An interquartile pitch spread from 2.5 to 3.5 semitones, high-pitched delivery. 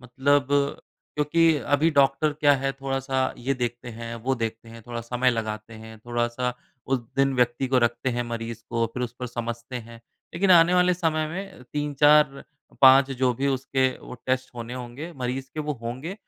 No: average, 3.2 semitones; low, 130 Hz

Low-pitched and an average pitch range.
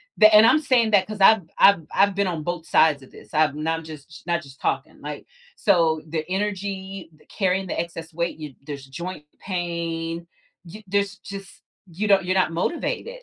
No: medium, 175 Hz; average, 3.6 semitones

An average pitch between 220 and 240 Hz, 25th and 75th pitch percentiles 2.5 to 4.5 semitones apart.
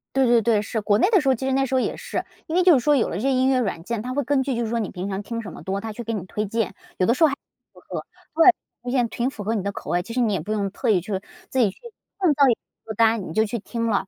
Yes: high, 230 Hz; average, 4.2 semitones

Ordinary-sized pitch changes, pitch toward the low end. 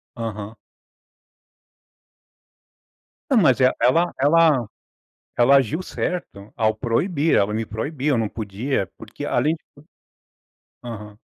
No: wide, 5.9 semitones; low, 125 Hz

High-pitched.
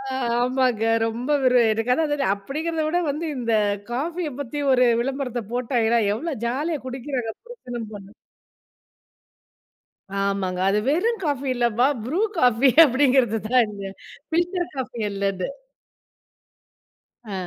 Yes: very high, 250 Hz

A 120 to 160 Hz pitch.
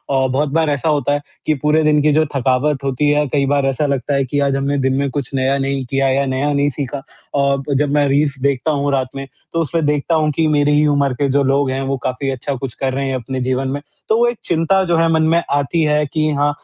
Yes: medium, 140 Hz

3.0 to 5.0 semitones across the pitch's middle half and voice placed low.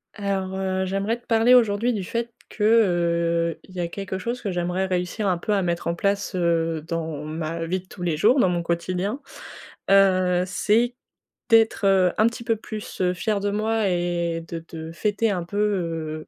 No: average, 3.5 semitones; high, 190 Hz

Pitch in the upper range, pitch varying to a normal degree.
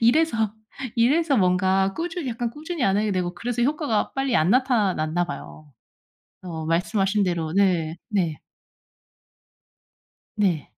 No: high, 200 Hz; wide, 5.7 semitones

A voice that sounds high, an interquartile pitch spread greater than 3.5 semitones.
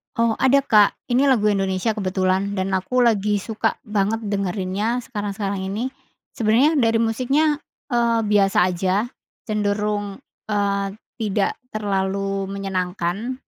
No: high, 205 Hz; average, 2.7 semitones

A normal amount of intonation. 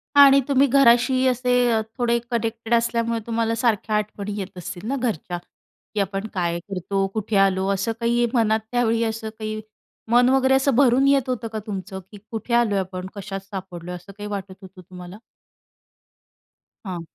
Yes: average, 3.6 semitones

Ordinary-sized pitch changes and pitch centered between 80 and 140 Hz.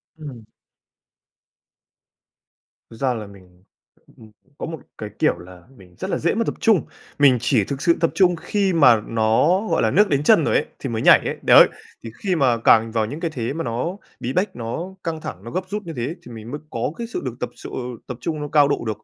No: wide, 6.6 semitones; low, 135 Hz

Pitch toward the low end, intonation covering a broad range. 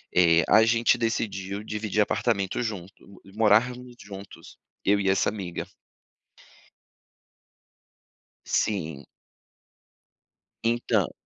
No: low, 105 Hz; average, 2.8 semitones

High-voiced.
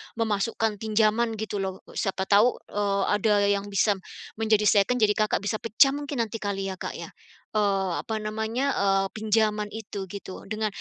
Yes: high, 210 Hz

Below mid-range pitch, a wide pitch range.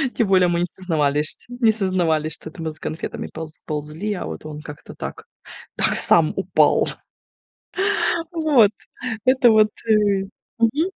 No: medium, 185 Hz; wide, 5.9 semitones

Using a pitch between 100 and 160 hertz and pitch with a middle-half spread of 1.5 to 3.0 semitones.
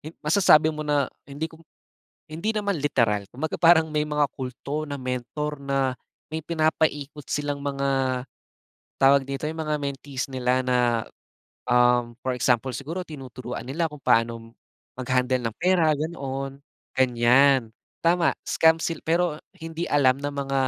No: medium, 140 Hz; average, 3.4 semitones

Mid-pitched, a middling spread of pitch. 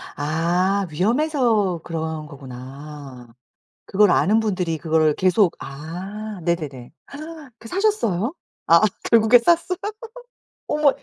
No: medium, 180 Hz; wide, 6.3 semitones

